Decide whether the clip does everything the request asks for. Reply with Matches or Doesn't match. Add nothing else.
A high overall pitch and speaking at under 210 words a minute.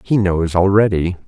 Doesn't match